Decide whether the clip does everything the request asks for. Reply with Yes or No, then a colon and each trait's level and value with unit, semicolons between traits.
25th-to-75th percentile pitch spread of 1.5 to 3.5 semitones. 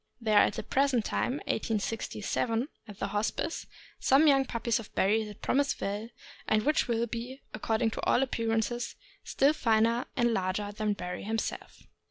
Yes: narrow, 2.6 semitones